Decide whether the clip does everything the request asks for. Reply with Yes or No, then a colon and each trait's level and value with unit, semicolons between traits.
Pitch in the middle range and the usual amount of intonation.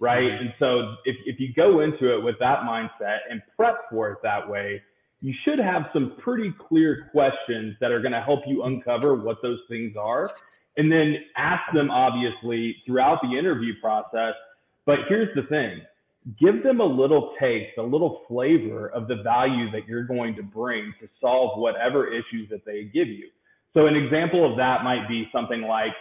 No: low, 125 Hz; average, 4.7 semitones